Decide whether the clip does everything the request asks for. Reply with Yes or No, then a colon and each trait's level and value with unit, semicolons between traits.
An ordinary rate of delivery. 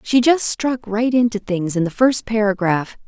Yes: average, 195 wpm